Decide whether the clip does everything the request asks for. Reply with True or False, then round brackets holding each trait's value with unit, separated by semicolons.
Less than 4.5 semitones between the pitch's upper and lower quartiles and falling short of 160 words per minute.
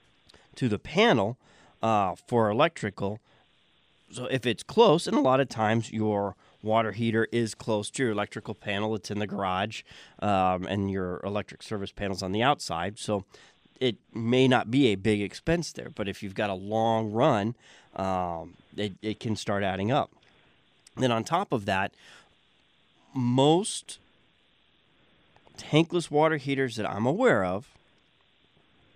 True (3.7 semitones; 150 wpm)